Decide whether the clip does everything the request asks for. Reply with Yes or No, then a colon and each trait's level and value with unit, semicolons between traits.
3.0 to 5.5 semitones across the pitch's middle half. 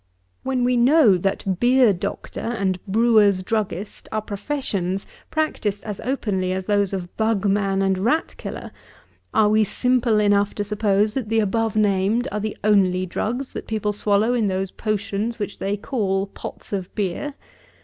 No: narrow, 2.6 semitones